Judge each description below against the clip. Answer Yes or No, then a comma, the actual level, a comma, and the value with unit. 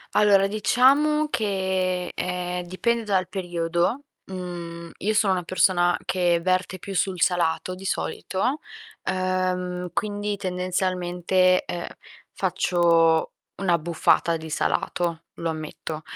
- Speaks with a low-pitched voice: No, medium, 185 Hz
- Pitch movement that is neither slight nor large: No, narrow, 1.8 semitones